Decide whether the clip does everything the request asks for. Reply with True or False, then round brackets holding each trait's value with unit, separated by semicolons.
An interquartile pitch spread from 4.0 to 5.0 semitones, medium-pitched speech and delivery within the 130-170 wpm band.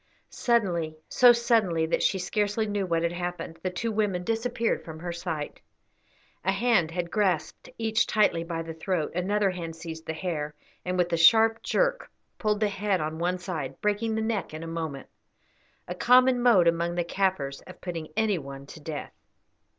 False (4.5 semitones; 180 Hz; 180 wpm)